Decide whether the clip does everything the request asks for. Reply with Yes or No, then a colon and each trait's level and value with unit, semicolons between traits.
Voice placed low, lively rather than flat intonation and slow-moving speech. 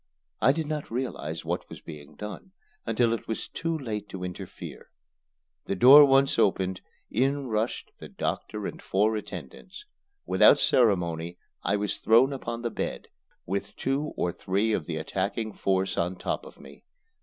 No: low, 110 Hz; wide, 5.9 semitones; average, 160 wpm